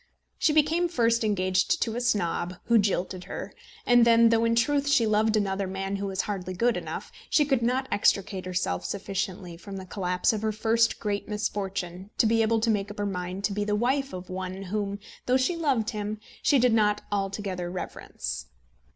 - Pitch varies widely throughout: No, average, 3.4 semitones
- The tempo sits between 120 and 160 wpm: No, average, 195 wpm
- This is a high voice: Yes, high, 210 Hz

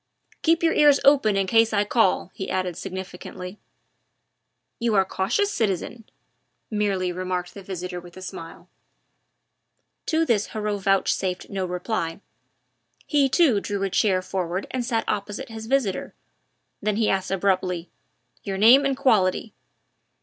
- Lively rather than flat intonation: No, average, 3.6 semitones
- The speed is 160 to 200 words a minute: No, average, 140 wpm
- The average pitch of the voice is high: Yes, high, 200 Hz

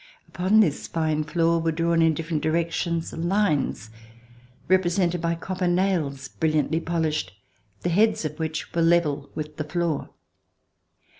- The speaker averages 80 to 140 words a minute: Yes, slow, 135 wpm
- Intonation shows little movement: Yes, narrow, 2.0 semitones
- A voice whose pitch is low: No, medium, 165 Hz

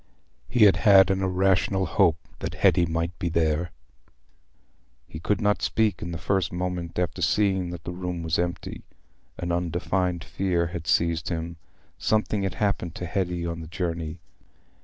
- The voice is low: Yes, very low, 90 Hz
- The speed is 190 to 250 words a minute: No, average, 160 wpm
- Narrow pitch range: Yes, narrow, 2.3 semitones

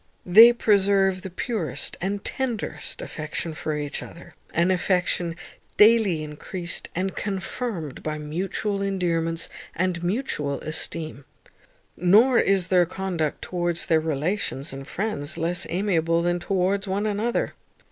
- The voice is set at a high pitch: No, medium, 180 Hz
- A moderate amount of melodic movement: Yes, average, 3.4 semitones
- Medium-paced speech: No, slow, 125 wpm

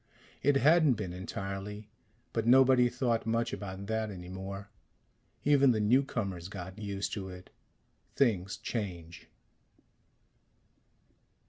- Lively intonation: No, average, 4.3 semitones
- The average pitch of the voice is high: No, low, 105 Hz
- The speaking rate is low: Yes, slow, 110 wpm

